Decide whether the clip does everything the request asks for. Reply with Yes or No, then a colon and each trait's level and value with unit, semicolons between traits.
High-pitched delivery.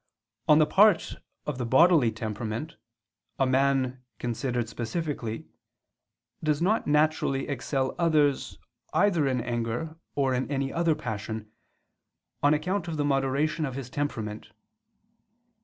No: low, 135 Hz